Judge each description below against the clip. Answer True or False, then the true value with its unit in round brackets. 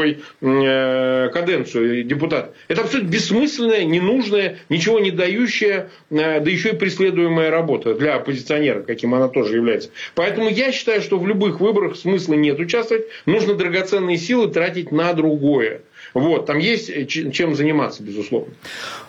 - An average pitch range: False (5.8 semitones)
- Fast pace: False (130 wpm)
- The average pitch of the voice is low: False (170 Hz)